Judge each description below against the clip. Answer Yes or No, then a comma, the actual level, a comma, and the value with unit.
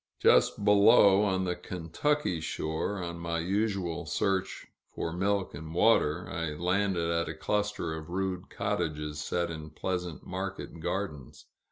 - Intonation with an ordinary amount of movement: Yes, average, 3.3 semitones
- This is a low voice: Yes, very low, 90 Hz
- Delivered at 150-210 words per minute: No, average, 140 wpm